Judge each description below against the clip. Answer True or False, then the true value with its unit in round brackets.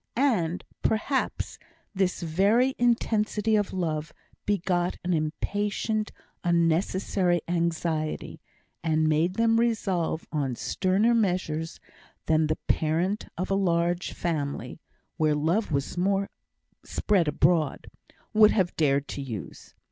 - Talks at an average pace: False (110 wpm)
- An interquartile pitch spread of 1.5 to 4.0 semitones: False (4.4 semitones)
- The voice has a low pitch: False (175 Hz)